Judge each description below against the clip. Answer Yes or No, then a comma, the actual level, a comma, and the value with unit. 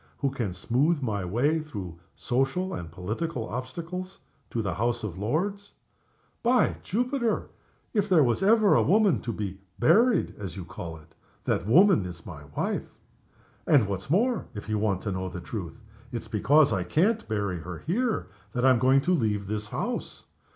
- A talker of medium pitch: No, low, 120 Hz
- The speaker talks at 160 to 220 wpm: Yes, average, 170 wpm